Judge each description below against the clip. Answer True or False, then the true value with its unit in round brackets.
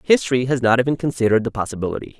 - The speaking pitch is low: True (125 Hz)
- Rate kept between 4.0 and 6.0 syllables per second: False (8.2 syllables/s)